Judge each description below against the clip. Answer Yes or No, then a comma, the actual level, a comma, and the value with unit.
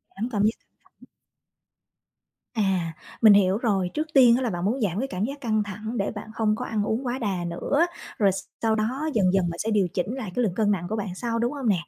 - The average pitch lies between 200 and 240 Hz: Yes, high, 215 Hz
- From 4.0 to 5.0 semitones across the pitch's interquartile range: No, average, 3.6 semitones